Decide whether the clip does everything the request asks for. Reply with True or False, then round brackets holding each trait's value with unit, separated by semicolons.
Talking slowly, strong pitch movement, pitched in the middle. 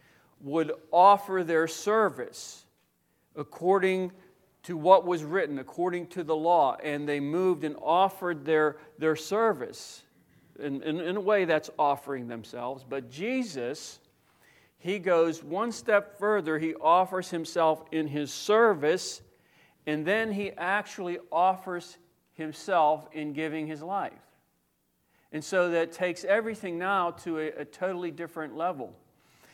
False (130 wpm; 3.6 semitones; 170 Hz)